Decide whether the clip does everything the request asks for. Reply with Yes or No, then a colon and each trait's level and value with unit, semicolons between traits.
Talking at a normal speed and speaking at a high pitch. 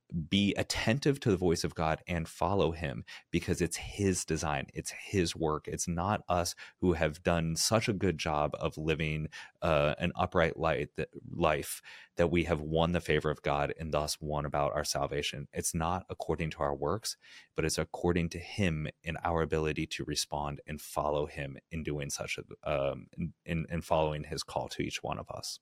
No: average, 195 wpm; very low, 80 Hz